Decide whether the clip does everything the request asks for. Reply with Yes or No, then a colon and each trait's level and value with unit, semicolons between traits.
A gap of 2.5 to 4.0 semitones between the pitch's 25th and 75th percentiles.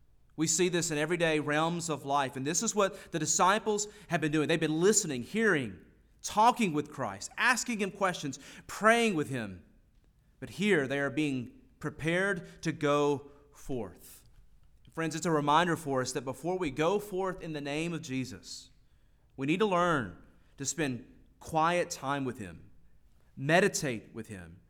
No: average, 5.0 semitones